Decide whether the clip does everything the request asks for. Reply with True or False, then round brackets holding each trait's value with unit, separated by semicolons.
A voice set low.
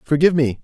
False (145 Hz)